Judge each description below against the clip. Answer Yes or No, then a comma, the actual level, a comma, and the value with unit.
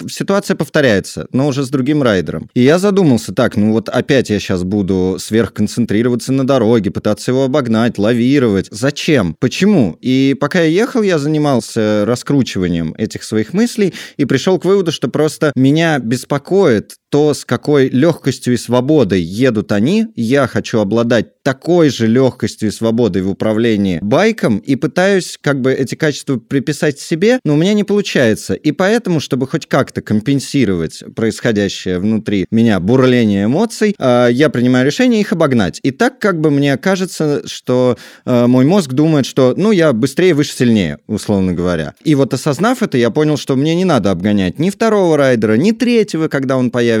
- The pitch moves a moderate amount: No, wide, 6.1 semitones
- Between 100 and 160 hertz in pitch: Yes, low, 135 Hz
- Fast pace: Yes, fast, 165 wpm